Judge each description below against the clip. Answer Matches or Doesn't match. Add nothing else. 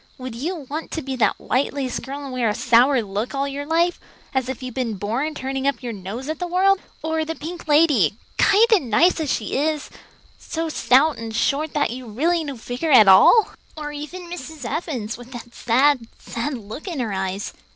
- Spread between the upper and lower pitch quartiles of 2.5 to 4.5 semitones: Doesn't match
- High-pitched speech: Matches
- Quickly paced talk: Matches